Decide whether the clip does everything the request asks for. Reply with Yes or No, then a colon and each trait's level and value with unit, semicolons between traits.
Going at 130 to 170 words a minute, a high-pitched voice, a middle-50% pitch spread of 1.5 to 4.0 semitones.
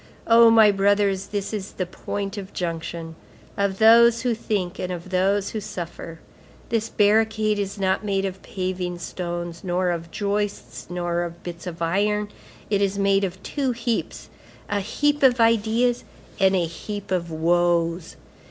Yes: average, 160 wpm; high, 195 Hz; average, 3.2 semitones